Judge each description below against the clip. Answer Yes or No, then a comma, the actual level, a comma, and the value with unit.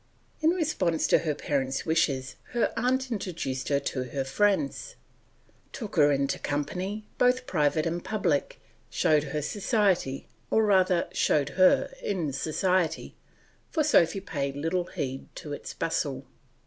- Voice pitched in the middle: Yes, medium, 165 Hz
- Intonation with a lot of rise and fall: Yes, wide, 6.3 semitones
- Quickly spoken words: No, slow, 135 wpm